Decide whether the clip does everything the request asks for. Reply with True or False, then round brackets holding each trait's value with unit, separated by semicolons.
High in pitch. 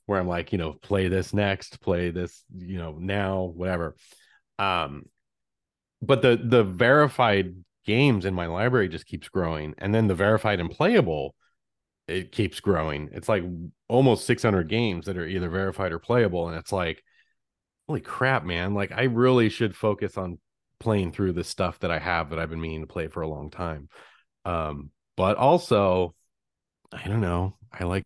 False (95 Hz)